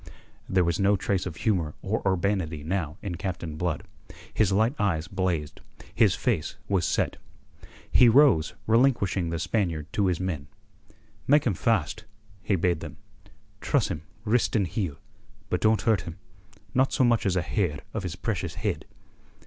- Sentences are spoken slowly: No, average, 165 wpm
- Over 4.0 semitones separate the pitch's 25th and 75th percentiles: Yes, average, 4.6 semitones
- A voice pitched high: No, very low, 95 Hz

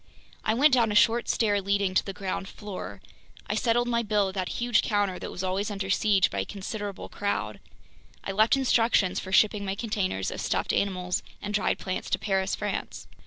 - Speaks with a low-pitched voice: No, high, 205 Hz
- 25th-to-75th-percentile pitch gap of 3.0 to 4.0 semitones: No, narrow, 2.4 semitones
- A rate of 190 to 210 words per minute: Yes, average, 200 wpm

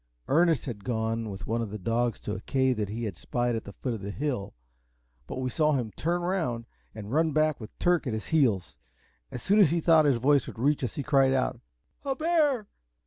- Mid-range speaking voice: No, low, 130 Hz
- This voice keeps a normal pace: No, fast, 230 wpm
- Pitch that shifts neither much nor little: No, wide, 5.8 semitones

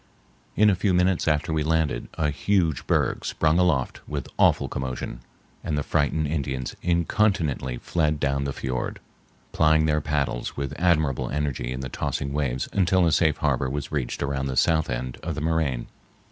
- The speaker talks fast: No, average, 175 wpm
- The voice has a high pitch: No, very low, 75 Hz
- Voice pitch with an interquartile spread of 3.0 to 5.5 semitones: Yes, average, 3.3 semitones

